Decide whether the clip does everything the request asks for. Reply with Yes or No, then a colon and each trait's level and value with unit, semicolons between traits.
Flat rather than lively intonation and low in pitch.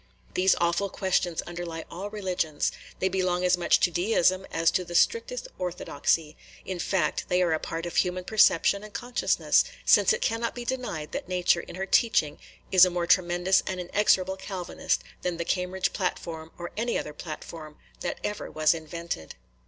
No: narrow, 2.2 semitones; medium, 180 Hz